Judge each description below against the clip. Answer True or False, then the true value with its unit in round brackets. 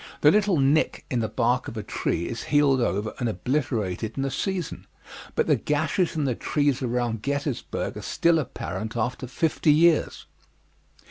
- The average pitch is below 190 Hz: True (135 Hz)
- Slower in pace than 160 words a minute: False (170 wpm)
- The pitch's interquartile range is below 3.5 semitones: False (4.7 semitones)